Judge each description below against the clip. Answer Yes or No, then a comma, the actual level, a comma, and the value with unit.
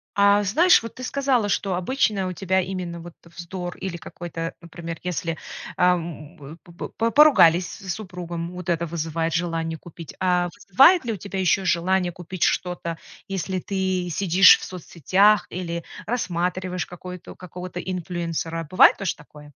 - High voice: No, medium, 180 Hz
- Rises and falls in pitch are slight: Yes, narrow, 2.1 semitones